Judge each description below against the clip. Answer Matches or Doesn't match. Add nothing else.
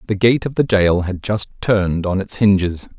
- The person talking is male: Matches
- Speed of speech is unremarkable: Doesn't match